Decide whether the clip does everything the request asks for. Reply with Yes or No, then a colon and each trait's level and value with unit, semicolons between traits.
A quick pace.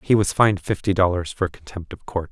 Yes: fast, 235 wpm